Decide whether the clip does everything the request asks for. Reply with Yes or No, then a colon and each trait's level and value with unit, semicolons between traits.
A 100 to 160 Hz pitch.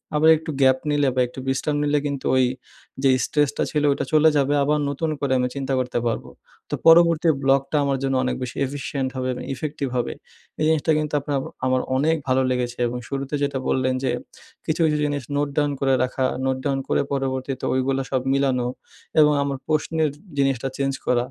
Yes: low, 135 Hz